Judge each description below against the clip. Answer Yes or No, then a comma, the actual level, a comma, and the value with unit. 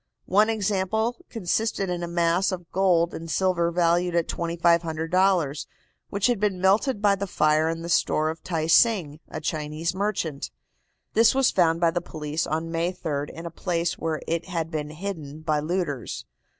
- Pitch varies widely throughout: No, average, 3.0 semitones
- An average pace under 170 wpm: No, average, 175 wpm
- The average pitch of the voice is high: No, medium, 170 Hz